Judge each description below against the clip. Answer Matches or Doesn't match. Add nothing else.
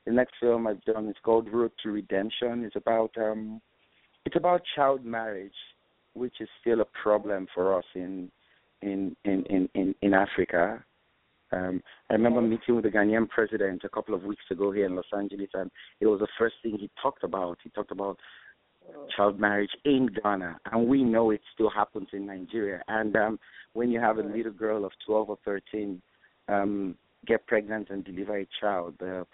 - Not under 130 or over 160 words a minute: Doesn't match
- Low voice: Matches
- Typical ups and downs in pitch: Doesn't match